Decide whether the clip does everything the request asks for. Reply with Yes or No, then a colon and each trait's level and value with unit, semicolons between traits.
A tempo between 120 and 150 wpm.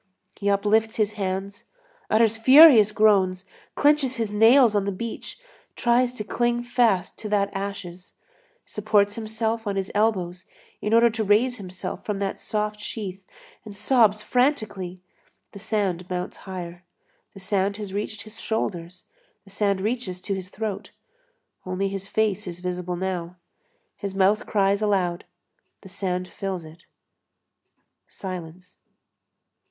Yes: slow, 135 wpm